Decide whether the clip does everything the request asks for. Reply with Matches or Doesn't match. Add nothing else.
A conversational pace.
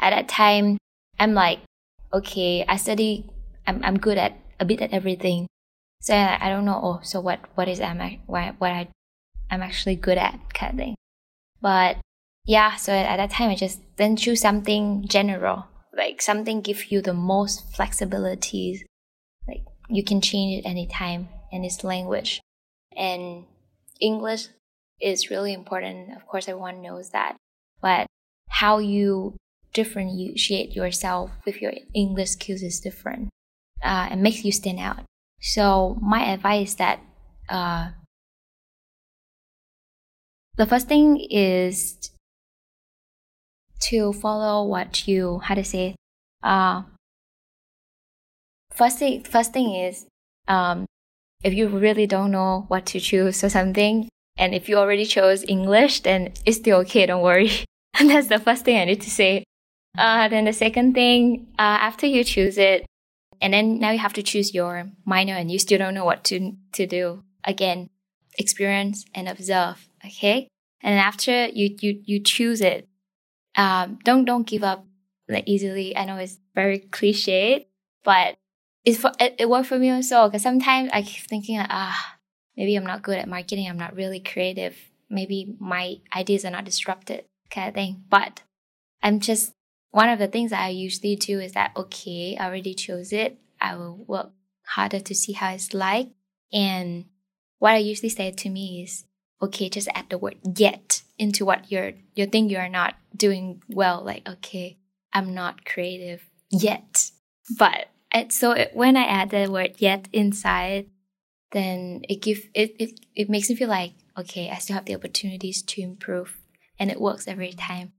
Matches